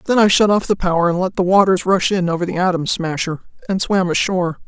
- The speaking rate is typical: No, fast, 245 wpm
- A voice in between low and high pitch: Yes, medium, 180 Hz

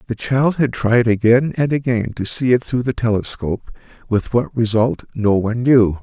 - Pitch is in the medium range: No, low, 120 Hz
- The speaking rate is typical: Yes, average, 190 wpm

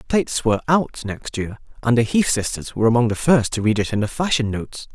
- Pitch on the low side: Yes, low, 120 Hz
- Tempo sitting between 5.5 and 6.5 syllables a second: Yes, 6.0 syllables/s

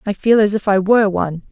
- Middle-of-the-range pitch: No, high, 205 Hz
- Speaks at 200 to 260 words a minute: No, fast, 280 wpm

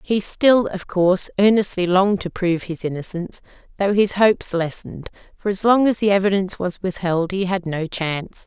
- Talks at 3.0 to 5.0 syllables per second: No, 5.5 syllables/s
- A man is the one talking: No, female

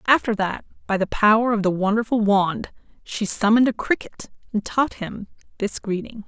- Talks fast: No, average, 170 wpm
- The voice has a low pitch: No, high, 215 Hz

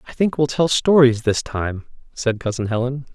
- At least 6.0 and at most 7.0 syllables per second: No, 4.9 syllables/s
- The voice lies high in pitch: No, low, 130 Hz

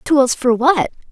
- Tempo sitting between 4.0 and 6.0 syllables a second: No, 3.6 syllables/s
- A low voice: No, very high, 265 Hz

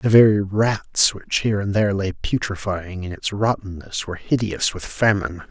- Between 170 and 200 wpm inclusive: Yes, average, 175 wpm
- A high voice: No, low, 100 Hz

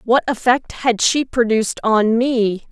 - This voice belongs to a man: No, female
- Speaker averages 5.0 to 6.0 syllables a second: No, 4.0 syllables/s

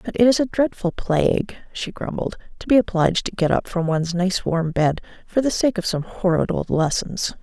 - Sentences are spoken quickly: Yes, fast, 220 wpm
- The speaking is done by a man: No, female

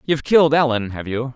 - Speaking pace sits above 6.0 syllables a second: Yes, 6.7 syllables/s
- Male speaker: Yes, male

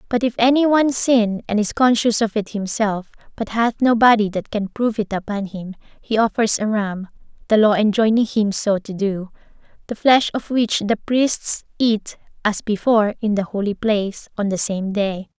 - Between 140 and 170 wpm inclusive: No, average, 185 wpm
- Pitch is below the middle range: No, high, 215 Hz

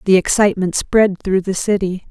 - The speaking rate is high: No, average, 170 wpm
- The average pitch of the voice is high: Yes, high, 195 Hz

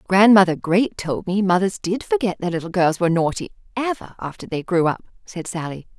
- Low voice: No, high, 190 Hz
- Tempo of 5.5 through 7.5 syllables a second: Yes, 5.6 syllables/s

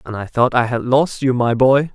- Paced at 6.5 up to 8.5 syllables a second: No, 4.9 syllables/s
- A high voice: No, low, 125 Hz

